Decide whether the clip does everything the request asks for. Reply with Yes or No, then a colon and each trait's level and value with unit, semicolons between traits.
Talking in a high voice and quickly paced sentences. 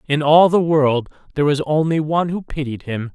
No: medium, 150 Hz; fast, 210 wpm